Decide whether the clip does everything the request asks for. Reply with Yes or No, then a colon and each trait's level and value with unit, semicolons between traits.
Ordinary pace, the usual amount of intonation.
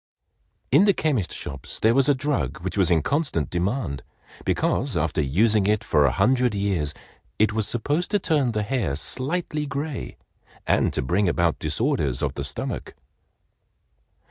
No: average, 160 wpm; wide, 8.6 semitones